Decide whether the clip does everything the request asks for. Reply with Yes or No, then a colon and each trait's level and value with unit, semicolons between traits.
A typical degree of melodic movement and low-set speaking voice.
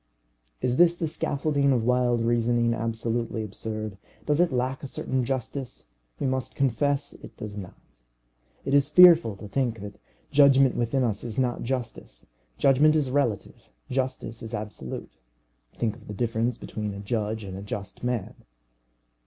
Yes: average, 3.8 semitones; low, 120 Hz